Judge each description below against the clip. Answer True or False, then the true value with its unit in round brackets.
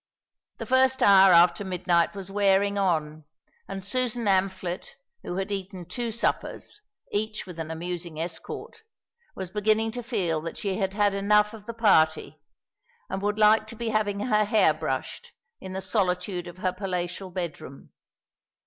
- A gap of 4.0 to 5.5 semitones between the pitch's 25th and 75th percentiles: False (3.1 semitones)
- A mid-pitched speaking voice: False (195 Hz)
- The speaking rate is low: False (160 wpm)